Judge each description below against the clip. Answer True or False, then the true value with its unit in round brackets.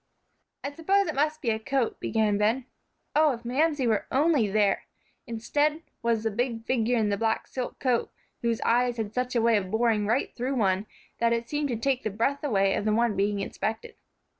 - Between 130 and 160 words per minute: False (205 wpm)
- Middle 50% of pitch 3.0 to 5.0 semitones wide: True (3.6 semitones)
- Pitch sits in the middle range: False (235 Hz)